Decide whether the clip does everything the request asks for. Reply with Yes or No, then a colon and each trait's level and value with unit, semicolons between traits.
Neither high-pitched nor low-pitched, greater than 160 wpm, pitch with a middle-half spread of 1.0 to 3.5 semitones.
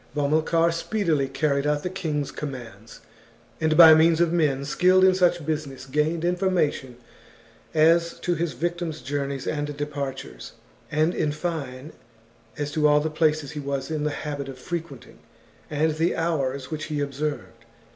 No: medium, 150 Hz; average, 155 wpm; average, 2.9 semitones